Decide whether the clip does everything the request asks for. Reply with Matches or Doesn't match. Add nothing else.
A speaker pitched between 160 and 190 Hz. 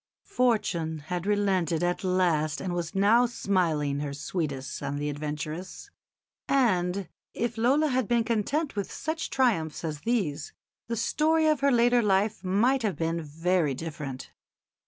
Matches